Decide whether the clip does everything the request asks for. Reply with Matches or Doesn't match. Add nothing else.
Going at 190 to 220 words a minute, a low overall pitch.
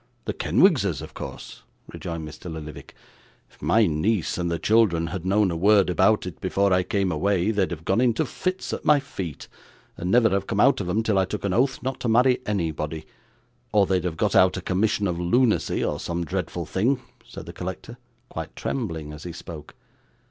Matches